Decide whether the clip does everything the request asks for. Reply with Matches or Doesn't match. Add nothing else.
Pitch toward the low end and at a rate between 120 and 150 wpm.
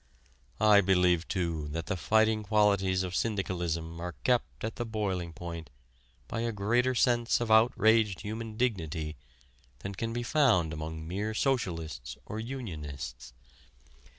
Matches